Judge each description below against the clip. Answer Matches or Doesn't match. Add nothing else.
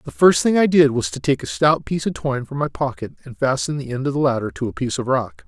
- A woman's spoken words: Doesn't match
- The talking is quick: Matches